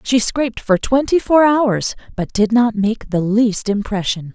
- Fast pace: No, average, 180 wpm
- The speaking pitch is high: Yes, high, 225 Hz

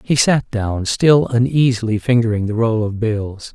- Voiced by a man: Yes, male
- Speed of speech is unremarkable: Yes, average, 170 wpm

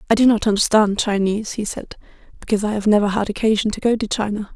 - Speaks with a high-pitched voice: Yes, high, 210 Hz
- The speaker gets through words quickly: Yes, fast, 225 wpm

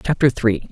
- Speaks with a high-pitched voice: No, low, 120 Hz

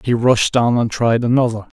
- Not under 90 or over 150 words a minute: No, average, 200 wpm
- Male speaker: Yes, male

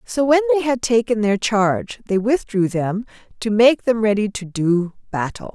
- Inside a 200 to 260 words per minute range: No, average, 185 wpm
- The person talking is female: Yes, female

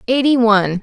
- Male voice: No, female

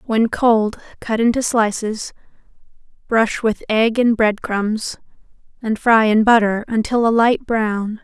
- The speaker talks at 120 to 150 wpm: Yes, average, 140 wpm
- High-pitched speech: Yes, high, 225 Hz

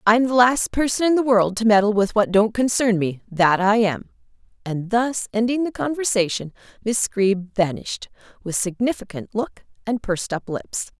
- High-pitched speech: Yes, high, 215 Hz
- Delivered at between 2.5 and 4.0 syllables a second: No, 5.0 syllables/s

